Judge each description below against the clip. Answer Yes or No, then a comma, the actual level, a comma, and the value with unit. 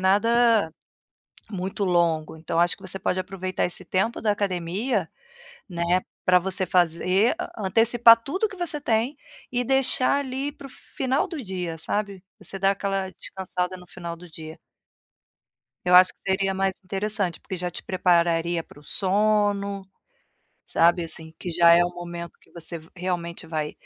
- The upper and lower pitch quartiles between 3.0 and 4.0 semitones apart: Yes, average, 3.4 semitones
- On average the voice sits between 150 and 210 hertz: Yes, medium, 185 Hz